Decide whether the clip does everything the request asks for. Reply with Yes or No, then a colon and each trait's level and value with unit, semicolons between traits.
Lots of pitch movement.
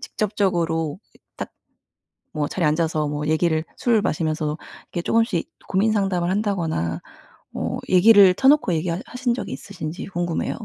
No: average, 4.5 semitones